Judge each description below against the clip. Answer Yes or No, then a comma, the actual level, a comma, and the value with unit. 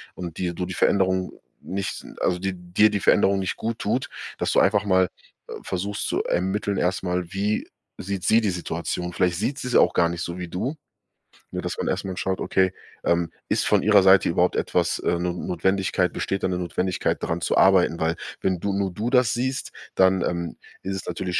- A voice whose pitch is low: Yes, very low, 95 Hz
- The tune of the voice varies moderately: No, narrow, 2.0 semitones